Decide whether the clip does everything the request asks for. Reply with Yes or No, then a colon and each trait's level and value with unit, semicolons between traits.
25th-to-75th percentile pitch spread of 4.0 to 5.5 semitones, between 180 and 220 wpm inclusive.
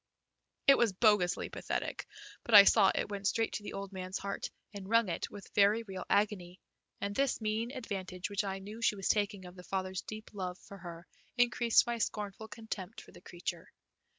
No: average, 2.8 semitones; average, 195 wpm